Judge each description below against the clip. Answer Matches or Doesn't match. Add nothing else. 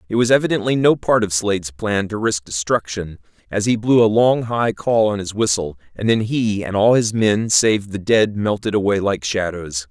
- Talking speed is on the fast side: Matches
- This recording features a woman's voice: Doesn't match